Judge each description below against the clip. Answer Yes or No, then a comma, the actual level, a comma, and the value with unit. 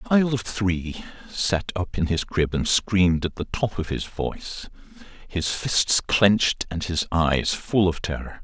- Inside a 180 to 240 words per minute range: Yes, average, 185 wpm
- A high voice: No, very low, 90 Hz